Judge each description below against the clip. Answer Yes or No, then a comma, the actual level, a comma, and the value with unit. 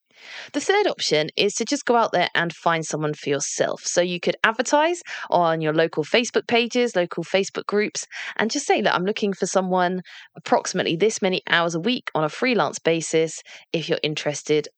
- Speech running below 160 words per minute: No, average, 195 wpm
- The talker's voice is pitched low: No, medium, 180 Hz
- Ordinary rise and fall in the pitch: No, wide, 6.0 semitones